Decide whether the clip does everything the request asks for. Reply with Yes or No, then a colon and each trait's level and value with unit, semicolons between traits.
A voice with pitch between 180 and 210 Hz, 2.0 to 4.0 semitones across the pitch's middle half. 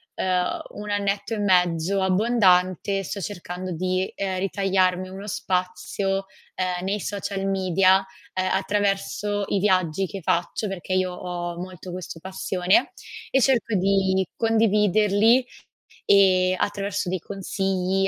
No: high, 190 Hz; narrow, 1.6 semitones